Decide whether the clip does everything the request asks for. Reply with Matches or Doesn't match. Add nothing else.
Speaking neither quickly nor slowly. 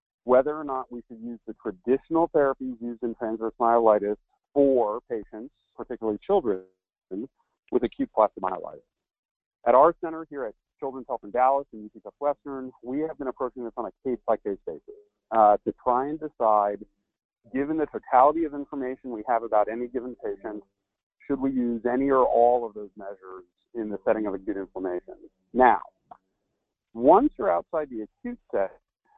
Matches